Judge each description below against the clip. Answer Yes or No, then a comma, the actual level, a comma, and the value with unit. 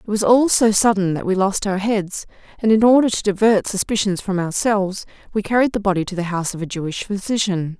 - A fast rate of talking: Yes, fast, 225 wpm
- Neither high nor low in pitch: No, high, 200 Hz